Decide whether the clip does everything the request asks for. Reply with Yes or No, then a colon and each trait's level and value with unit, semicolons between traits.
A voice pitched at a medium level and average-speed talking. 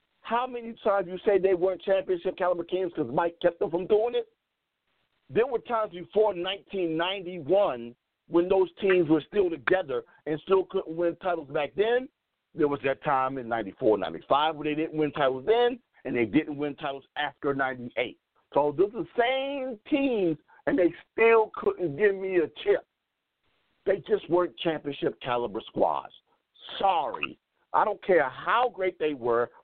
Yes: medium, 180 Hz; average, 165 wpm